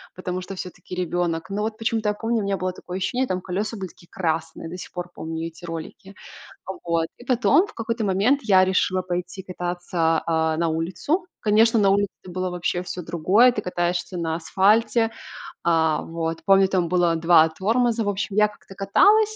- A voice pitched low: No, medium, 185 Hz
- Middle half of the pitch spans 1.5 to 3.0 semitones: No, average, 3.7 semitones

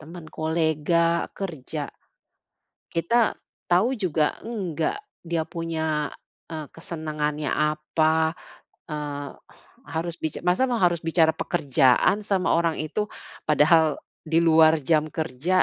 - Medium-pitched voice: Yes, medium, 160 Hz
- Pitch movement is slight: Yes, narrow, 2.1 semitones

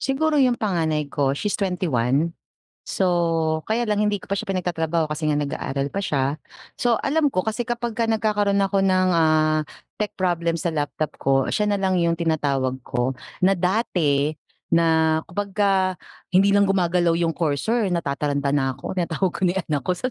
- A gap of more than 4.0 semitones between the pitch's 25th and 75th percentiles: Yes, average, 4.7 semitones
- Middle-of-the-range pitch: Yes, medium, 175 Hz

